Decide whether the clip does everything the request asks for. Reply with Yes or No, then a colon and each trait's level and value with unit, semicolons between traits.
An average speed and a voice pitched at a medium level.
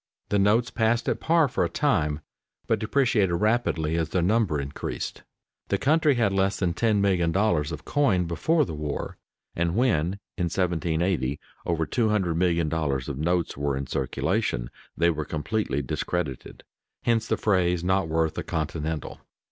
No: average, 150 wpm; very low, 85 Hz